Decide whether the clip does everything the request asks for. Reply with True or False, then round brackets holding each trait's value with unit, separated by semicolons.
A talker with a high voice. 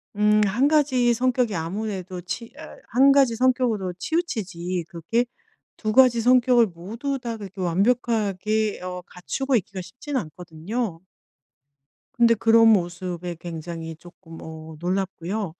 True (210 Hz)